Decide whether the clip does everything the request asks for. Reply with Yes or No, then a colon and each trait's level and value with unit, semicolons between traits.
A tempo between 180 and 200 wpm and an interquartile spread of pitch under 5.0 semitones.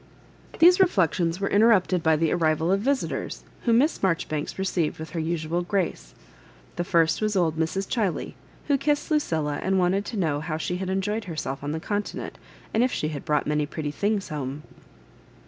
Yes: average, 190 wpm; average, 4.5 semitones